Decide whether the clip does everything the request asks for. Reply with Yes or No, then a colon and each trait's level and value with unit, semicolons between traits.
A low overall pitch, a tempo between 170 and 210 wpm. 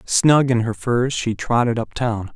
Yes: low, 120 Hz; fast, 205 wpm